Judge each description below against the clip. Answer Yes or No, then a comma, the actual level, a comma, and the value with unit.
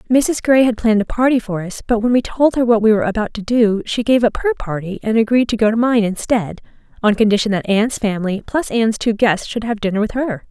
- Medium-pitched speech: No, high, 225 Hz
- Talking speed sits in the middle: No, fast, 255 wpm